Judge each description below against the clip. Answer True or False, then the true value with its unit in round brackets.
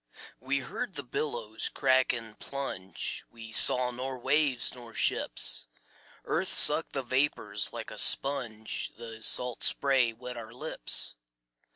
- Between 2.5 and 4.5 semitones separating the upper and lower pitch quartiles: True (3.0 semitones)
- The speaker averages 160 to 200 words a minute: False (135 wpm)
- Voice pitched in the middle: False (125 Hz)